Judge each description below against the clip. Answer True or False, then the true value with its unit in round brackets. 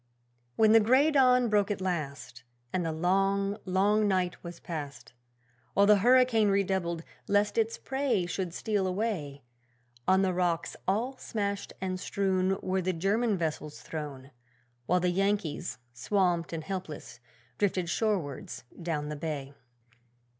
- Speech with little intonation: False (3.6 semitones)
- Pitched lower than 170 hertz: False (190 Hz)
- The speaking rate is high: False (140 wpm)